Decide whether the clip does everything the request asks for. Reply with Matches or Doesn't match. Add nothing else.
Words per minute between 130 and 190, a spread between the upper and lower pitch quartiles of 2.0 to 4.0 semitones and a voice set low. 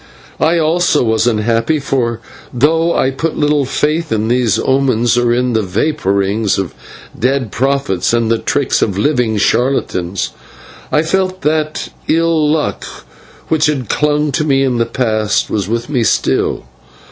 Doesn't match